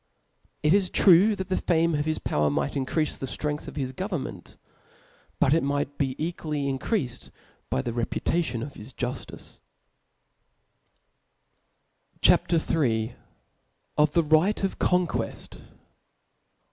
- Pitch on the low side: No, medium, 150 Hz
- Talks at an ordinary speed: No, slow, 110 wpm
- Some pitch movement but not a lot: Yes, average, 4.5 semitones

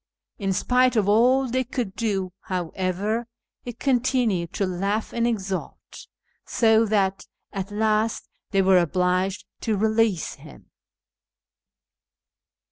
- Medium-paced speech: No, slow, 120 wpm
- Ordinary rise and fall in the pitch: Yes, average, 3.4 semitones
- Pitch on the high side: Yes, high, 210 Hz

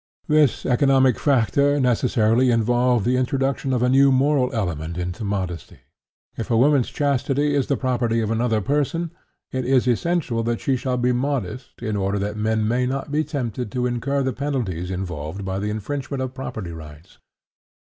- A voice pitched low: Yes, low, 125 Hz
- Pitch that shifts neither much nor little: Yes, average, 4.0 semitones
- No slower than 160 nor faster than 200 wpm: Yes, average, 170 wpm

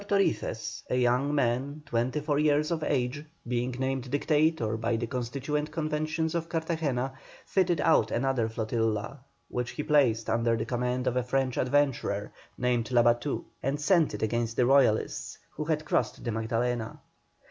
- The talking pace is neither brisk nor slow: Yes, average, 155 wpm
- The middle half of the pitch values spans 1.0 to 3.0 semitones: No, average, 4.1 semitones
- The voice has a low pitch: Yes, low, 130 Hz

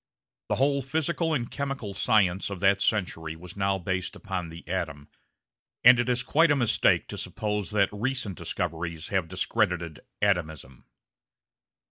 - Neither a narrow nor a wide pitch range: No, wide, 5.7 semitones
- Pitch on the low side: Yes, low, 100 Hz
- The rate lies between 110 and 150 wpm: Yes, average, 145 wpm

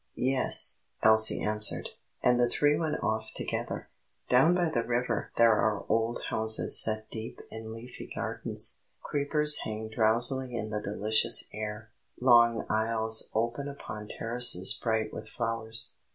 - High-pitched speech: No, low, 115 Hz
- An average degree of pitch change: No, narrow, 2.0 semitones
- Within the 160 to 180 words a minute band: No, average, 140 wpm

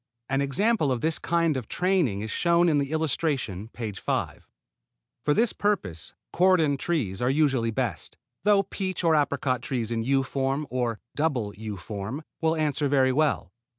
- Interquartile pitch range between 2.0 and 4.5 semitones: No, wide, 5.6 semitones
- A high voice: No, medium, 140 Hz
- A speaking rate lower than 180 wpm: Yes, average, 165 wpm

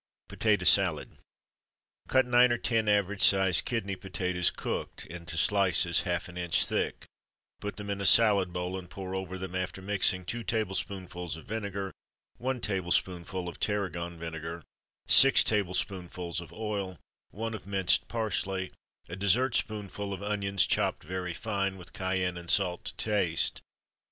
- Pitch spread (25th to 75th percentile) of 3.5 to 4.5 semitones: No, narrow, 2.6 semitones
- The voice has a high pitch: No, very low, 95 Hz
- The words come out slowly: No, average, 150 wpm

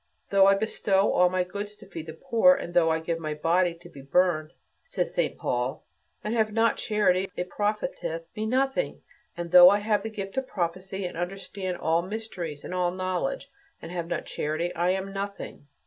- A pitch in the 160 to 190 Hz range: Yes, medium, 185 Hz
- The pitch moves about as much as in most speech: Yes, average, 3.3 semitones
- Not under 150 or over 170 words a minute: No, average, 195 wpm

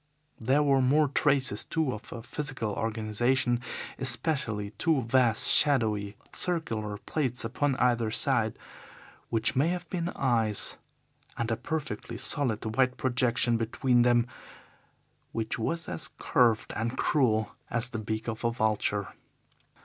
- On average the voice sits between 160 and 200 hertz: No, low, 120 Hz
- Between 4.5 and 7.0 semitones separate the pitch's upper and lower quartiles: No, average, 3.5 semitones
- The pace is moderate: No, slow, 130 wpm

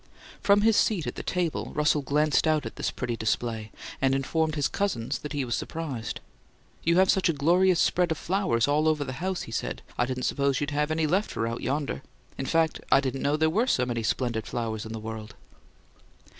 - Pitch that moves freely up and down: No, average, 5.0 semitones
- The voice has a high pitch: No, medium, 145 Hz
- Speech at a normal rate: No, fast, 210 wpm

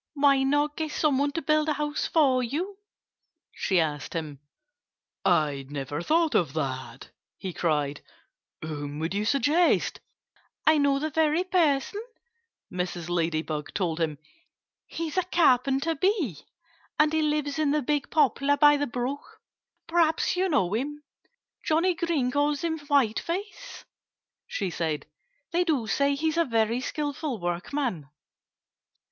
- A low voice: No, very high, 280 Hz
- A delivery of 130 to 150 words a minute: Yes, average, 140 wpm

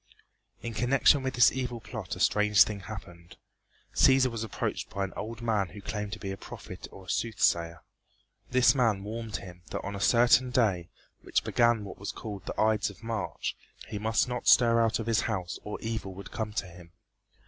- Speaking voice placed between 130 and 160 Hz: No, low, 110 Hz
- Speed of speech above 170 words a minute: Yes, average, 200 wpm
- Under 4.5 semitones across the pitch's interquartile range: Yes, average, 3.0 semitones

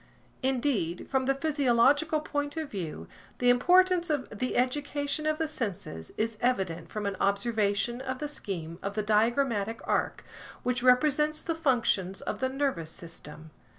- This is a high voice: Yes, very high, 250 Hz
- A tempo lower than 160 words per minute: Yes, average, 150 wpm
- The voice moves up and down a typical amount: No, wide, 6.2 semitones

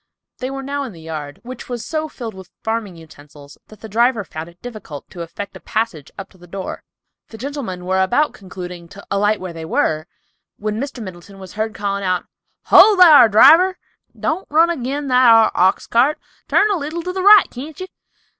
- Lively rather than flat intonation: Yes, wide, 7.2 semitones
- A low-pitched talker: No, high, 220 Hz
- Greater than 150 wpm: Yes, average, 200 wpm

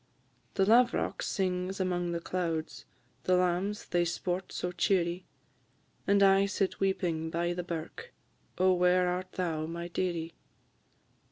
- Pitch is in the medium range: Yes, medium, 180 Hz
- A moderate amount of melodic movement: No, narrow, 1.7 semitones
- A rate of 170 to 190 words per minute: No, slow, 135 wpm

